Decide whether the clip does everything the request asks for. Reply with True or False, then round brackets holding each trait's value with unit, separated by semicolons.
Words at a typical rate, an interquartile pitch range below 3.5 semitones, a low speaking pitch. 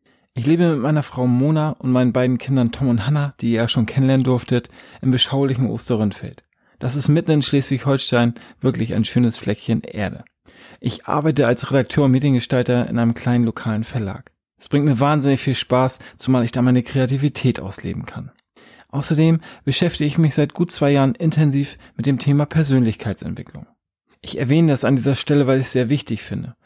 True (180 wpm; 2.9 semitones; 130 Hz)